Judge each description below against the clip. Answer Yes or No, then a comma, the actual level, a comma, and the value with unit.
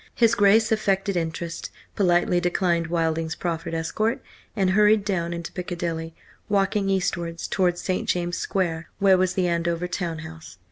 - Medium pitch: Yes, medium, 175 Hz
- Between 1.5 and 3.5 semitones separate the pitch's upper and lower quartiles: Yes, narrow, 2.5 semitones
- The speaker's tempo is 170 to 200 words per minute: No, average, 145 wpm